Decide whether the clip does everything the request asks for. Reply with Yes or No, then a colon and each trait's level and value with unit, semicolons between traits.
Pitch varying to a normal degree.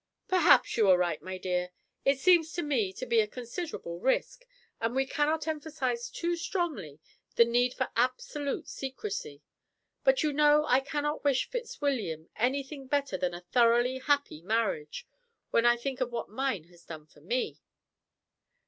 No: wide, 6.6 semitones